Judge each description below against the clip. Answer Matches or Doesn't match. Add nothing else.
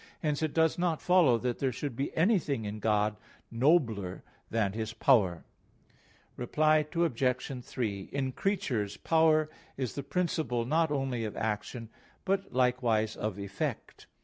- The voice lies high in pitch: Doesn't match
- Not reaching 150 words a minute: Matches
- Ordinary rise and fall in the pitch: Doesn't match